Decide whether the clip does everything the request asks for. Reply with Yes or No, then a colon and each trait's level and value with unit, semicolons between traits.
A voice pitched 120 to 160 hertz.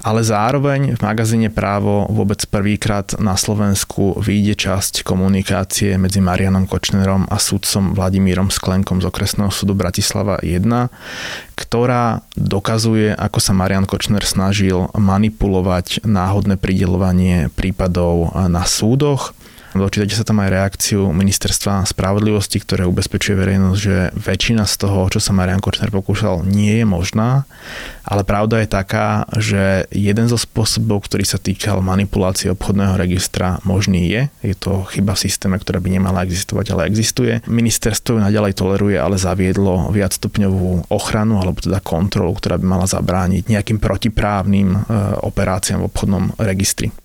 No: low, 100 Hz